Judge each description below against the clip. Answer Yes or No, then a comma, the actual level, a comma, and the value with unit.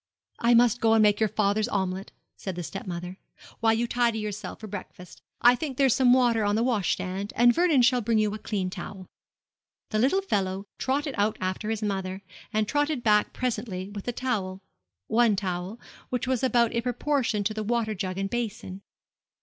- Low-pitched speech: No, high, 215 Hz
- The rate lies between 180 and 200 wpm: Yes, average, 190 wpm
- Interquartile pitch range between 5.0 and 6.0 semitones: No, average, 3.6 semitones